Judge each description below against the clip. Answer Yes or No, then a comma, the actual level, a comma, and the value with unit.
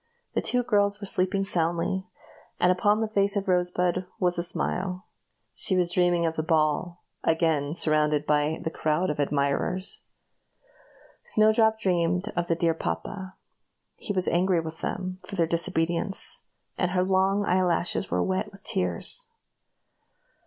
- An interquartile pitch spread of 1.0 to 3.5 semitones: Yes, average, 2.8 semitones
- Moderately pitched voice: Yes, medium, 180 Hz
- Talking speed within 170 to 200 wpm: No, average, 150 wpm